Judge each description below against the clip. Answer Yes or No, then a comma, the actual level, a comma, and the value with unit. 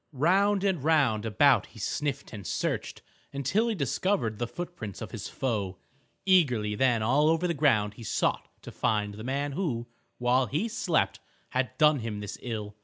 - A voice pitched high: No, low, 130 Hz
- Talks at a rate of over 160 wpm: Yes, average, 175 wpm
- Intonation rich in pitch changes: Yes, wide, 6.5 semitones